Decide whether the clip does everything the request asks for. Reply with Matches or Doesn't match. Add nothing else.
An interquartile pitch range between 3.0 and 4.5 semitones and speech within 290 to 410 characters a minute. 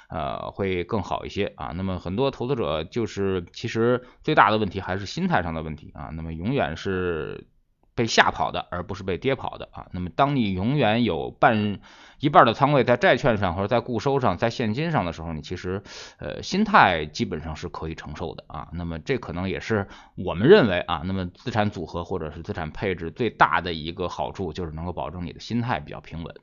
Doesn't match